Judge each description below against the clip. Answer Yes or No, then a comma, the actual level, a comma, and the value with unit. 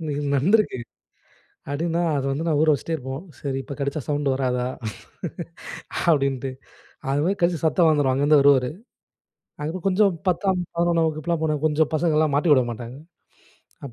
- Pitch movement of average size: Yes, average, 3.3 semitones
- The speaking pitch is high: No, medium, 150 Hz